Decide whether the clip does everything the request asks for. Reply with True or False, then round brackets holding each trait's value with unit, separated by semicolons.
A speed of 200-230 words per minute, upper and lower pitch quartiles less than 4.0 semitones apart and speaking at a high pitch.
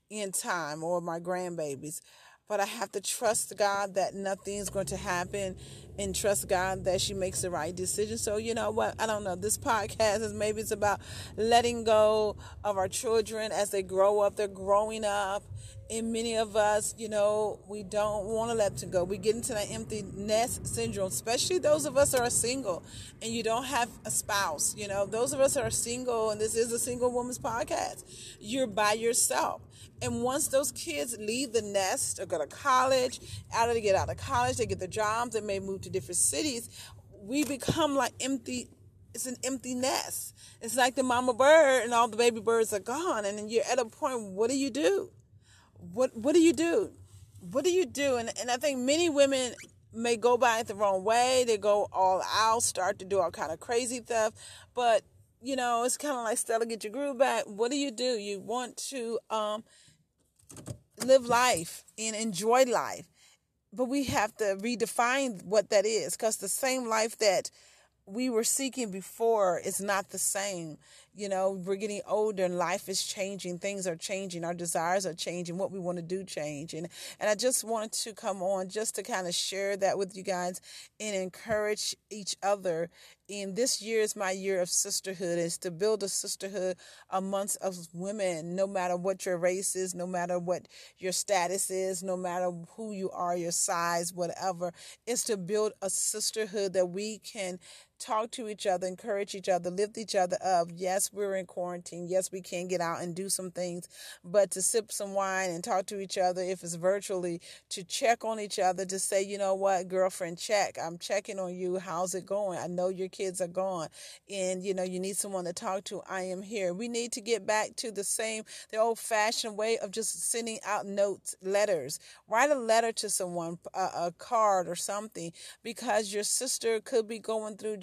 True (205 wpm; 3.6 semitones; 205 Hz)